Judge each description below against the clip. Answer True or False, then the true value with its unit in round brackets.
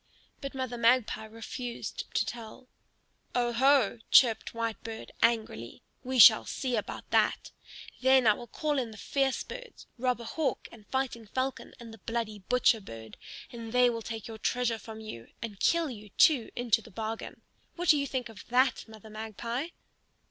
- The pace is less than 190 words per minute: True (165 wpm)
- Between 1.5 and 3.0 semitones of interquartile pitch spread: True (2.7 semitones)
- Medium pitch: False (235 Hz)